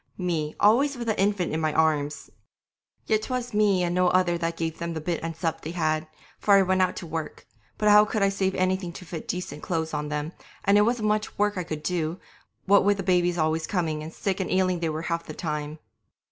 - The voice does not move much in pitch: No, average, 3.7 semitones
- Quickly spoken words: Yes, fast, 235 wpm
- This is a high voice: No, medium, 175 Hz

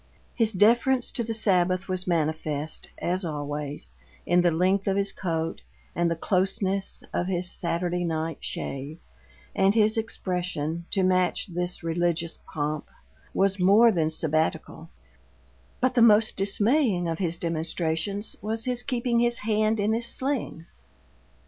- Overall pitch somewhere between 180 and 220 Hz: Yes, medium, 185 Hz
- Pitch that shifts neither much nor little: Yes, average, 4.5 semitones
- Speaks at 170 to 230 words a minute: No, average, 140 wpm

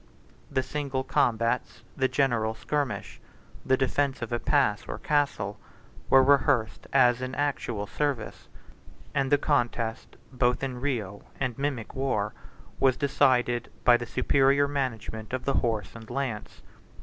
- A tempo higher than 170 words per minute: No, slow, 135 wpm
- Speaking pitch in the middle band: No, low, 130 Hz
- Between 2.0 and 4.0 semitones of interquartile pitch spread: Yes, average, 3.1 semitones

